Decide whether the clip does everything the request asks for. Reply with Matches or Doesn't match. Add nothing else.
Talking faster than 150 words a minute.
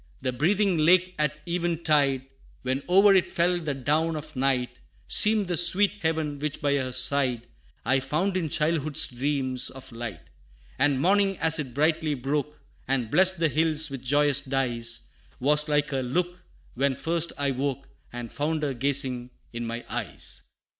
Matches